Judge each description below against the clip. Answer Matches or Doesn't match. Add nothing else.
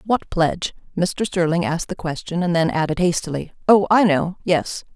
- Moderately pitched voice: Matches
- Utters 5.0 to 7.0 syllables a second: Matches